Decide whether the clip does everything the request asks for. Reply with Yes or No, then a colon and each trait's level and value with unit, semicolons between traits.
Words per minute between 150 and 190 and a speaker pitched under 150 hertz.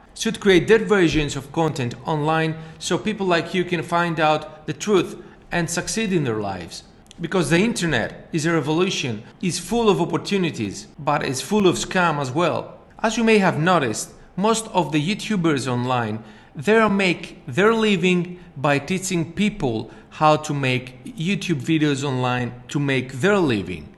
No: average, 165 wpm; medium, 170 Hz